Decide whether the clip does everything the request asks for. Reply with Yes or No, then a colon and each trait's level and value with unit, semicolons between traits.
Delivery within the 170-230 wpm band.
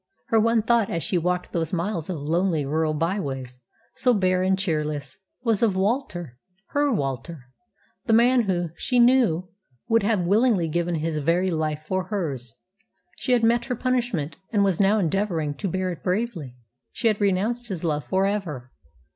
Yes: average, 175 wpm